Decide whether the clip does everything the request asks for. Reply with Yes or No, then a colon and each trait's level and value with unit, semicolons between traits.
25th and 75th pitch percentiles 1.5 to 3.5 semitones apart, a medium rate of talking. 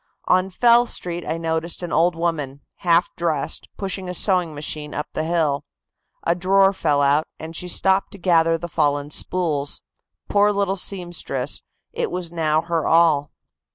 Yes: average, 2.9 semitones; average, 160 wpm